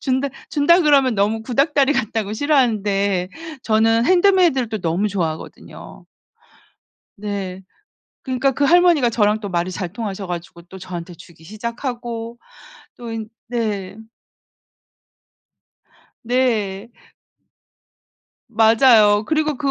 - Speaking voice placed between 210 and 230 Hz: Yes, high, 225 Hz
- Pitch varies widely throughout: No, average, 4.8 semitones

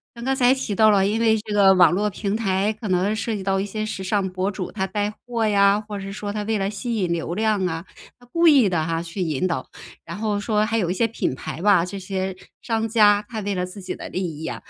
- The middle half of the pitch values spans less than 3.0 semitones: Yes, narrow, 2.6 semitones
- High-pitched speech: Yes, high, 205 Hz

